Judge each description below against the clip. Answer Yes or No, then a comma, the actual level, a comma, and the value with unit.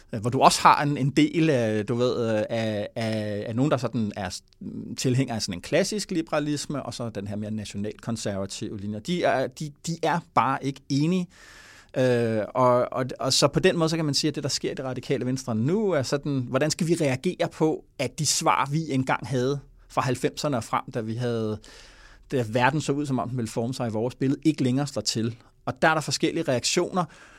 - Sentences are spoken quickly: Yes, fast, 225 wpm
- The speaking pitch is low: Yes, low, 130 Hz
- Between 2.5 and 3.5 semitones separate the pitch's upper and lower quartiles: No, average, 4.7 semitones